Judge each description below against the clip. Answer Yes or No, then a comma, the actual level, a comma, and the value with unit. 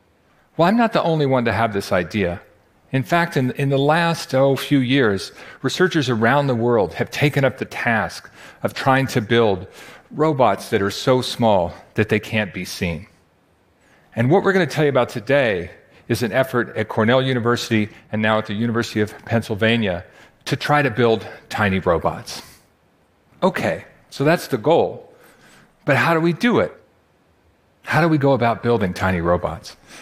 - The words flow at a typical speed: No, fast, 180 wpm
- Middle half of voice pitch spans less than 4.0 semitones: No, average, 4.8 semitones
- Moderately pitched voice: No, low, 125 Hz